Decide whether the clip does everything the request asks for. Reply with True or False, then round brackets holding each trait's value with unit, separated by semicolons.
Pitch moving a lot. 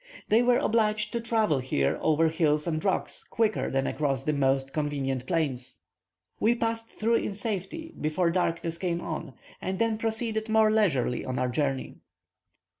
True (7.5 semitones)